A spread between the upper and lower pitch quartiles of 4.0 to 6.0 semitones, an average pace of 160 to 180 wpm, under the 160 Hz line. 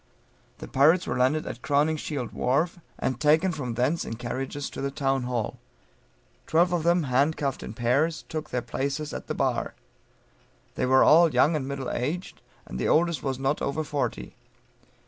No: average, 3.6 semitones; average, 165 wpm; medium, 140 Hz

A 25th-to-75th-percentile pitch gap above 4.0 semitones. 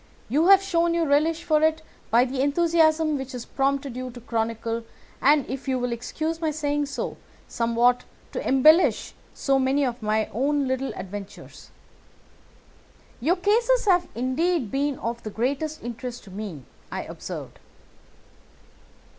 Yes: average, 4.8 semitones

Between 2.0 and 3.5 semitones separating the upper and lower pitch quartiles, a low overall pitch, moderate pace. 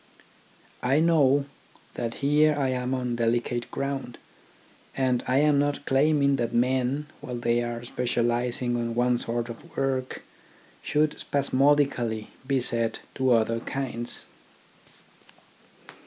No: average, 2.7 semitones; low, 125 Hz; slow, 120 wpm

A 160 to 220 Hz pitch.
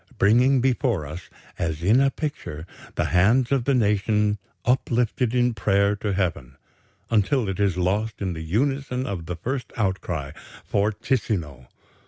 No: low, 105 Hz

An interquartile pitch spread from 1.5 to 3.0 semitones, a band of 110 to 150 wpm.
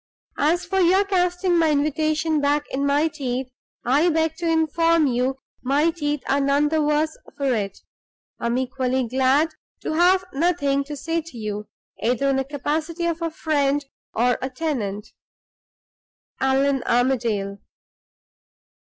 No: average, 3.6 semitones; average, 145 wpm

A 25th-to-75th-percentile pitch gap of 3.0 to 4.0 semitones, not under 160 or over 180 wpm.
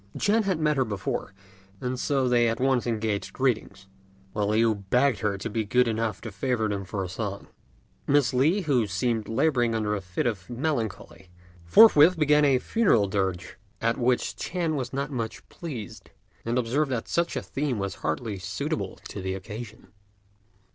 No: average, 5.1 semitones; average, 175 wpm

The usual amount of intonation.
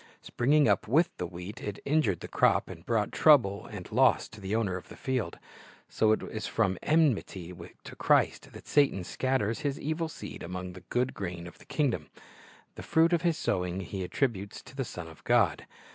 No: wide, 6.7 semitones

